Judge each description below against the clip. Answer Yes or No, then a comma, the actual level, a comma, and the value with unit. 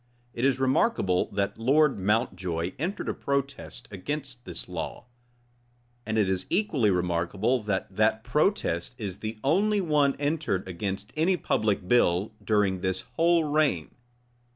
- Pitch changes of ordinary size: No, wide, 7.5 semitones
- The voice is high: No, low, 115 Hz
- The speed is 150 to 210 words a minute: No, slow, 135 wpm